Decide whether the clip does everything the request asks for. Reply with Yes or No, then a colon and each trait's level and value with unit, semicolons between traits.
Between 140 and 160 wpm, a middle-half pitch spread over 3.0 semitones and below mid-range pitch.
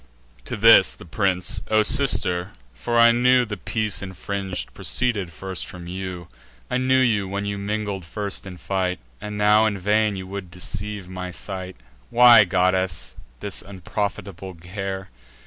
No: average, 145 wpm; narrow, 2.4 semitones; low, 100 Hz